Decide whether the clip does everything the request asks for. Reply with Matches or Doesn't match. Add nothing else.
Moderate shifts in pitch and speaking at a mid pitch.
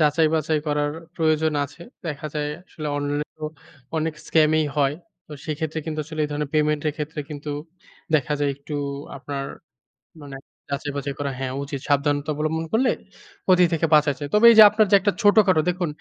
Doesn't match